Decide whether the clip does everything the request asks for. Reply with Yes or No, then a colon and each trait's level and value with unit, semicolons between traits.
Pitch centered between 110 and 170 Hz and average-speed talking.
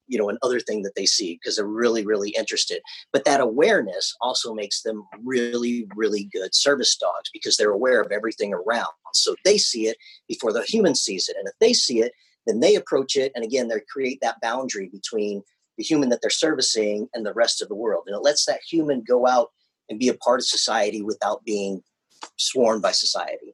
No: low, 135 Hz; fast, 210 wpm